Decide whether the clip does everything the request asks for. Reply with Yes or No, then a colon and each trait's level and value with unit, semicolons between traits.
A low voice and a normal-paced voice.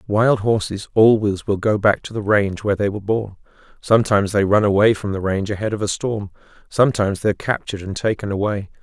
No: low, 105 Hz; fast, 210 wpm